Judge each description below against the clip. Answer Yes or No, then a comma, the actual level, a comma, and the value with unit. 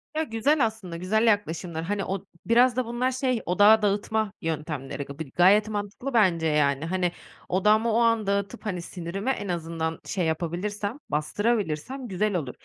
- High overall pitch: Yes, high, 200 Hz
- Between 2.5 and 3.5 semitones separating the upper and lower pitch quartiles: No, average, 4.9 semitones